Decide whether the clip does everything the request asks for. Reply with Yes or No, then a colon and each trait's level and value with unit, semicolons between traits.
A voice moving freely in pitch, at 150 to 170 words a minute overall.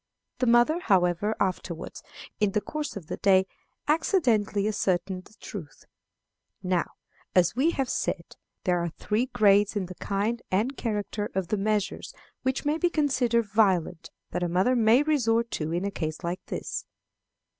No: average, 4.5 semitones; average, 160 wpm